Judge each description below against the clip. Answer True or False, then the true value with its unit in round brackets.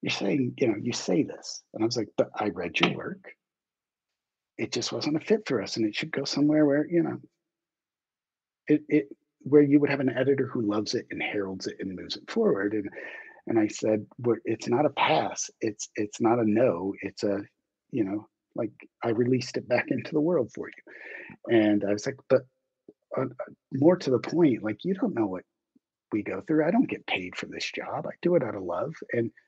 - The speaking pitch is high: False (130 Hz)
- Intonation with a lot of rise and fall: True (6.6 semitones)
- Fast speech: True (225 wpm)